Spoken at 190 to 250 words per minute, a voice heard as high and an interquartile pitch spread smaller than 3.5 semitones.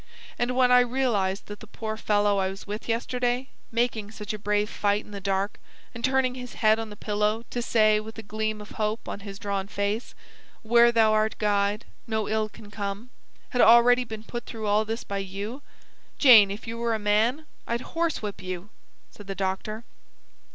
Yes: average, 195 wpm; high, 215 Hz; narrow, 2.4 semitones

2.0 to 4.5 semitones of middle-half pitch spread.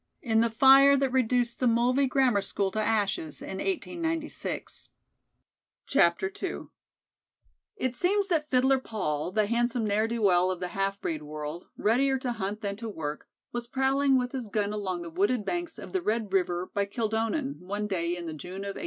No: wide, 5.4 semitones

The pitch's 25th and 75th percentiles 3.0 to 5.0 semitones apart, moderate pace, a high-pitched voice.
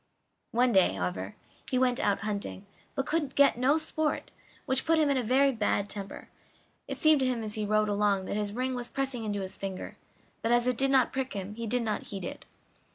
No: average, 4.5 semitones; fast, 220 wpm; high, 235 Hz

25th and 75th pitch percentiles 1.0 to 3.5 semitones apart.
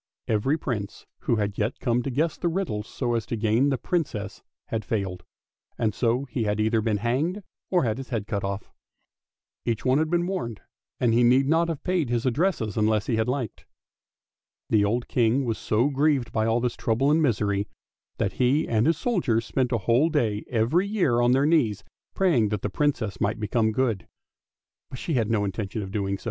No: average, 4.7 semitones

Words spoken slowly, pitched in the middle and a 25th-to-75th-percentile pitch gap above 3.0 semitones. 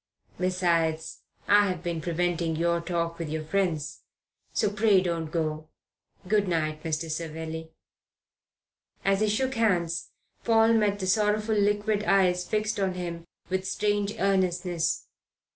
Yes: slow, 130 wpm; medium, 180 Hz; average, 3.7 semitones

